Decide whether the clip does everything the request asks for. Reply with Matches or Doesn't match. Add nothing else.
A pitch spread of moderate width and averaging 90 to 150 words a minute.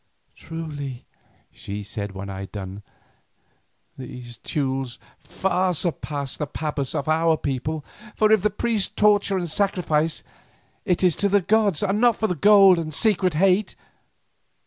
Doesn't match